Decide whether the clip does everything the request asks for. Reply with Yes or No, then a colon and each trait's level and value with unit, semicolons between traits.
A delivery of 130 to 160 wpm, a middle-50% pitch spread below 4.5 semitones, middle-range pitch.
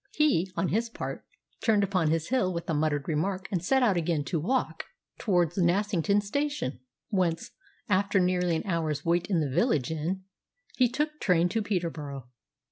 No: average, 170 wpm; average, 4.1 semitones; medium, 180 Hz